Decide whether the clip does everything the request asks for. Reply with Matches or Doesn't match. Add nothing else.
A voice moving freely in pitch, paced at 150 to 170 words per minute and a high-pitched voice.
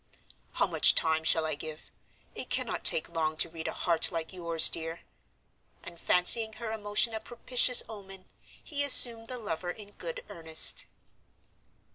Doesn't match